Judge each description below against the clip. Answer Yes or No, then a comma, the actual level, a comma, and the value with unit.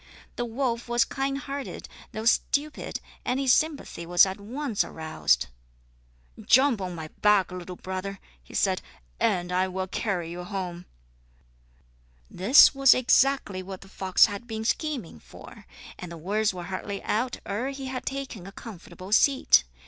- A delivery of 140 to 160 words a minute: Yes, average, 155 wpm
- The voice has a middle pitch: No, high, 205 Hz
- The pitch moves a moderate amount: No, wide, 6.0 semitones